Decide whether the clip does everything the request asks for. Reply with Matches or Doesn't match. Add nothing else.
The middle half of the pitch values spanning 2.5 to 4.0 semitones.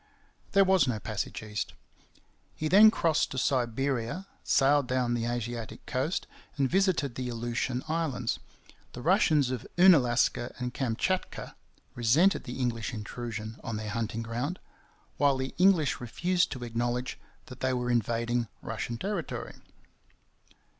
Doesn't match